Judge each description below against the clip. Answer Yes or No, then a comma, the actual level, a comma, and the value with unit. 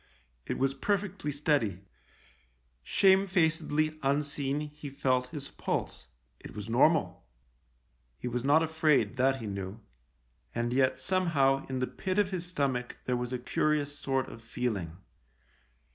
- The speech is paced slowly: No, average, 150 wpm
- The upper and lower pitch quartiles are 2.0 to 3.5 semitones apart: No, average, 4.0 semitones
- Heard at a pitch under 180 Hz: Yes, low, 135 Hz